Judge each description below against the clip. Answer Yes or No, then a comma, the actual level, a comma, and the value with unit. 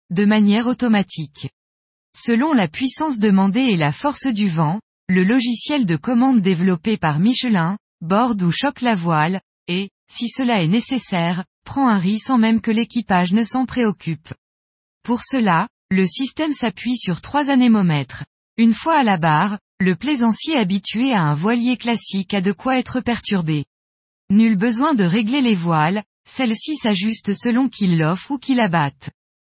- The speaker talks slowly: No, average, 160 wpm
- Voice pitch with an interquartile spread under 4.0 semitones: No, wide, 5.6 semitones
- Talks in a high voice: Yes, high, 215 Hz